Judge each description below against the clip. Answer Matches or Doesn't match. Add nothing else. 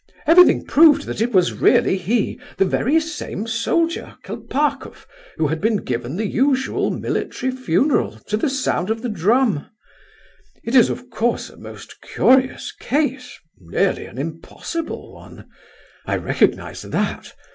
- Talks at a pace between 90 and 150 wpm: Matches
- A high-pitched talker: Matches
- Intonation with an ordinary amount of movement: Doesn't match